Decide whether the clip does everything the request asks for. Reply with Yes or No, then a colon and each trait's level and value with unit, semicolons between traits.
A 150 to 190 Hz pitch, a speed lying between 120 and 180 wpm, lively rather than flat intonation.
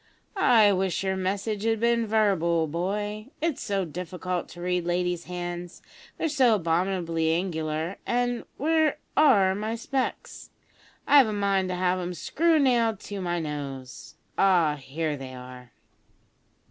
No: medium, 185 Hz; average, 140 wpm; average, 4.4 semitones